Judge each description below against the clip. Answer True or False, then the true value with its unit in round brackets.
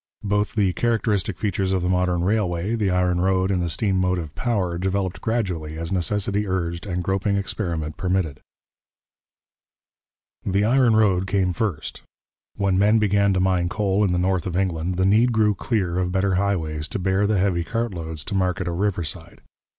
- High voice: False (95 Hz)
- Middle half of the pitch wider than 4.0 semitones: False (2.5 semitones)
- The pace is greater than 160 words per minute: True (175 wpm)